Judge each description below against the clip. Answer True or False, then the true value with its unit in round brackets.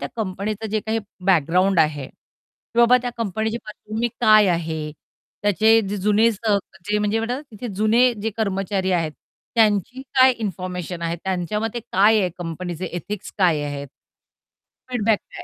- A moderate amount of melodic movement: True (3.8 semitones)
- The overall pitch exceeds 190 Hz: True (205 Hz)